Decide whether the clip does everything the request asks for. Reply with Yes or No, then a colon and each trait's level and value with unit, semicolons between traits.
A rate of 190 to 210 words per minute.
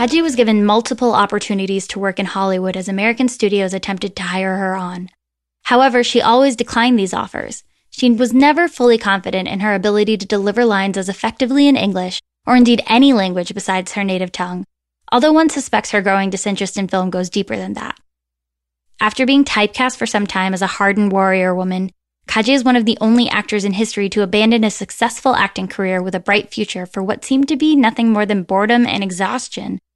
Yes: average, 200 wpm